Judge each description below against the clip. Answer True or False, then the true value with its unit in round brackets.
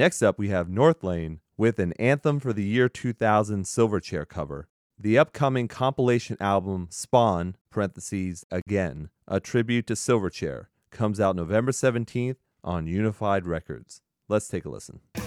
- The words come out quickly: False (140 wpm)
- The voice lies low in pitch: True (105 Hz)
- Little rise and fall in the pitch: False (4.8 semitones)